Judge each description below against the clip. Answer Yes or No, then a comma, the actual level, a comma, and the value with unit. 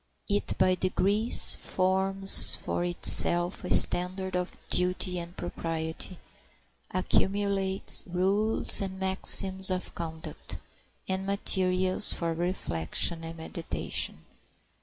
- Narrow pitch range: Yes, narrow, 1.7 semitones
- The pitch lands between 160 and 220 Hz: Yes, medium, 185 Hz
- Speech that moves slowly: Yes, slow, 95 wpm